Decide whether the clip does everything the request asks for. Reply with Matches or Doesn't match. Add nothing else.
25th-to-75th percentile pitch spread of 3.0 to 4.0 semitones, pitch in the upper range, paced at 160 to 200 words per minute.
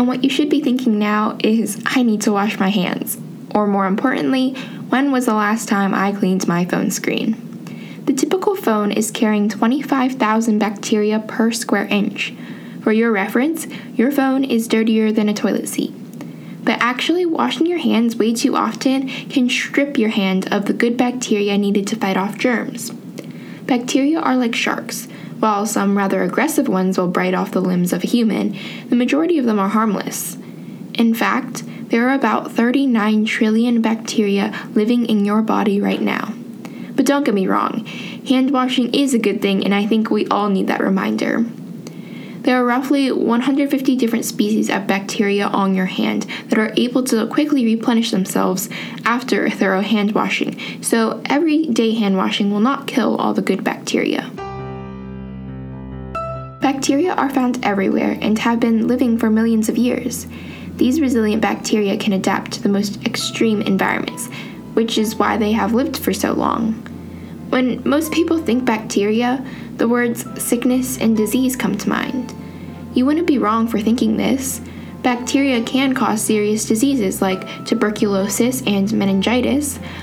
Matches